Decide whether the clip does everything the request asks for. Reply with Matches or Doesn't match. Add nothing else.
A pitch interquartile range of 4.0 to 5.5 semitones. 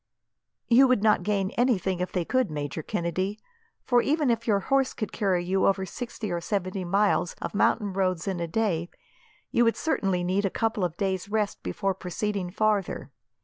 Doesn't match